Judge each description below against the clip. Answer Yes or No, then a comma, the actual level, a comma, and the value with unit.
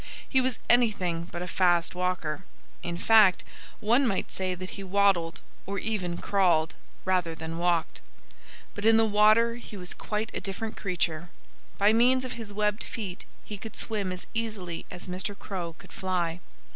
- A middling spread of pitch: Yes, average, 3.6 semitones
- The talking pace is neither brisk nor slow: Yes, average, 170 wpm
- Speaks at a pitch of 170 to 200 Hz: Yes, high, 190 Hz